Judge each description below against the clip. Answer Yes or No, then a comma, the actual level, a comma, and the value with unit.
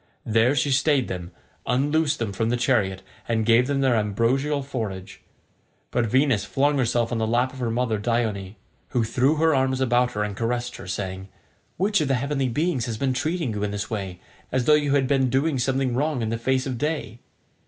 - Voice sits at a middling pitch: No, low, 125 Hz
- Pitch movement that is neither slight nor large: Yes, average, 3.5 semitones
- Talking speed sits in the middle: No, fast, 210 wpm